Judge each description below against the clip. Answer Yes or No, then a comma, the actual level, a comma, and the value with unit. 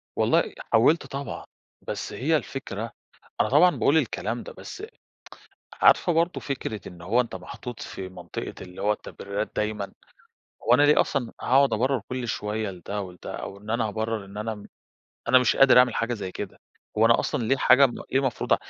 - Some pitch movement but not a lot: Yes, average, 4.3 semitones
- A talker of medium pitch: No, low, 115 Hz